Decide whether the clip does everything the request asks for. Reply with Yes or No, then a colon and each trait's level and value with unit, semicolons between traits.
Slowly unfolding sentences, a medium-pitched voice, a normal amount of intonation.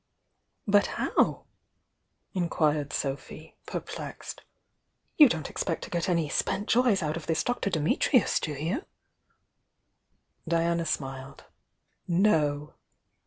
Yes: slow, 110 wpm; medium, 165 Hz; average, 4.4 semitones